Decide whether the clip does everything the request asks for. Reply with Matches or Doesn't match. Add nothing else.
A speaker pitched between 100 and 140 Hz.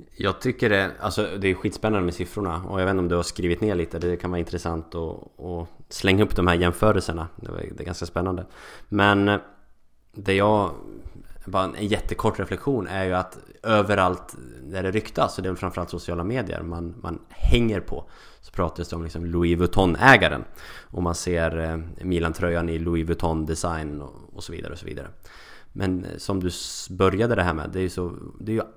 Doesn't match